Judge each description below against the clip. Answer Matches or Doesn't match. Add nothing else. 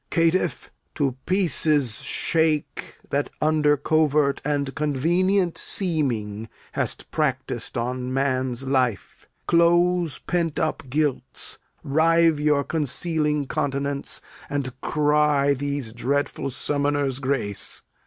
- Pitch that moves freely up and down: Doesn't match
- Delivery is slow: Matches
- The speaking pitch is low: Doesn't match